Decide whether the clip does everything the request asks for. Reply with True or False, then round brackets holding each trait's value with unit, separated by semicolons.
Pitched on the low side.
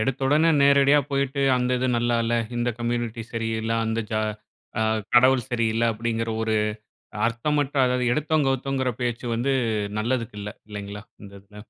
True (120 Hz)